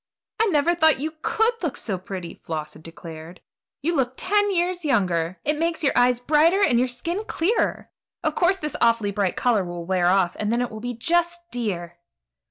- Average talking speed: Yes, average, 195 wpm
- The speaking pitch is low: No, high, 245 Hz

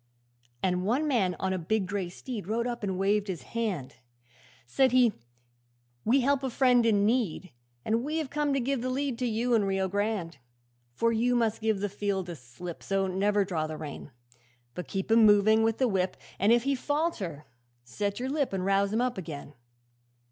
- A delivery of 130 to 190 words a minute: No, average, 200 wpm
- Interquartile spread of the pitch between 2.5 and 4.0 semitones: No, average, 4.5 semitones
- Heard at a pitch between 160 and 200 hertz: No, high, 210 Hz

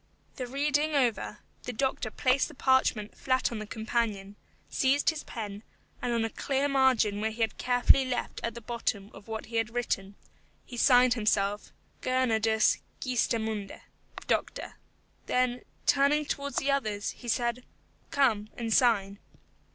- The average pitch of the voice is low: No, high, 240 Hz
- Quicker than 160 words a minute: No, average, 150 wpm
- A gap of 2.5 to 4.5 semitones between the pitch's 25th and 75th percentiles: Yes, average, 3.2 semitones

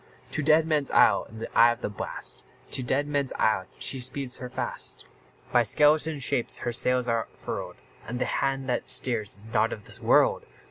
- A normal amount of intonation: Yes, average, 3.4 semitones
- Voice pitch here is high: No, low, 125 Hz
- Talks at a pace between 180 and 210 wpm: Yes, average, 185 wpm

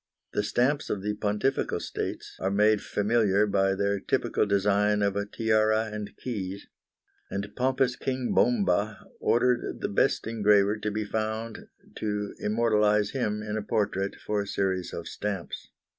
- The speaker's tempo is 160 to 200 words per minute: No, average, 150 wpm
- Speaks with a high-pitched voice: No, low, 105 Hz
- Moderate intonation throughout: No, narrow, 1.6 semitones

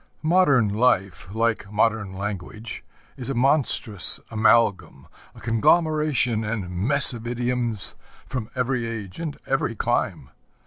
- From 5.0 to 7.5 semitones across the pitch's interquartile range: No, average, 3.7 semitones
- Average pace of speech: No, slow, 120 wpm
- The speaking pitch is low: Yes, low, 115 Hz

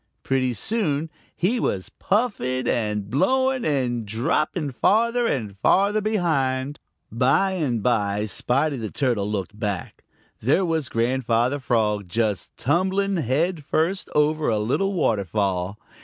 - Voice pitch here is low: Yes, low, 130 Hz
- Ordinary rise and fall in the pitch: No, wide, 8.0 semitones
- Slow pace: Yes, slow, 125 wpm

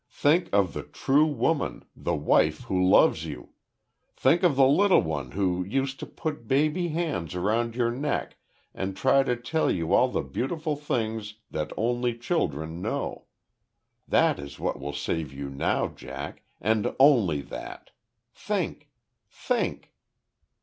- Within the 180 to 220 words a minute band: No, average, 145 wpm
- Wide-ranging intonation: Yes, wide, 8.8 semitones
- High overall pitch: No, low, 115 Hz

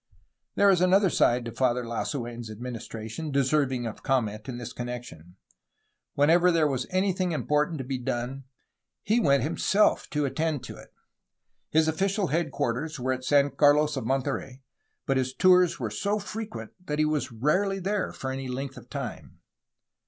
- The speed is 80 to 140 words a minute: No, average, 165 wpm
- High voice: No, medium, 140 Hz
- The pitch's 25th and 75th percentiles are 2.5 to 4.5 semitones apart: No, average, 5.0 semitones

